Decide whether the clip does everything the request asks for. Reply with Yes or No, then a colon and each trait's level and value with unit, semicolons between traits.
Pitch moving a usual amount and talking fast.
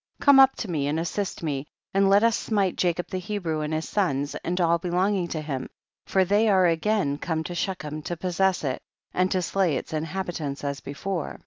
Yes: average, 3.8 semitones; fast, 215 wpm